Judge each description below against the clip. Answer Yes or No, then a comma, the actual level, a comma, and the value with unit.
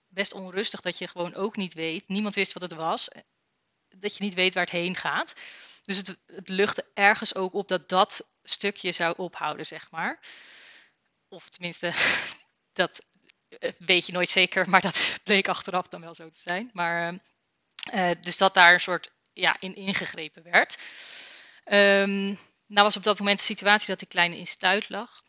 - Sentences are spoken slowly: No, average, 180 wpm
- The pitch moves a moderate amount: No, narrow, 2.2 semitones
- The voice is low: No, high, 190 Hz